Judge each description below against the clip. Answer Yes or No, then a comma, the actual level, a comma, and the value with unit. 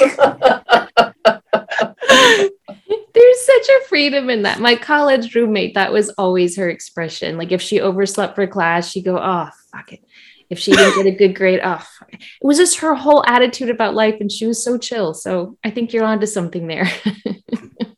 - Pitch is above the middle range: Yes, high, 220 Hz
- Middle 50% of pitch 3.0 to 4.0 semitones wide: No, average, 4.7 semitones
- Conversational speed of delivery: Yes, average, 180 wpm